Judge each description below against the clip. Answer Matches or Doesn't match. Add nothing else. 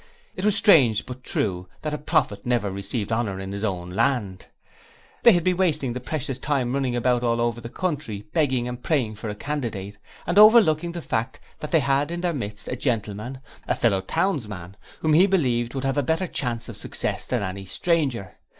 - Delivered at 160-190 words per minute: Doesn't match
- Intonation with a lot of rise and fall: Matches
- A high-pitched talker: Doesn't match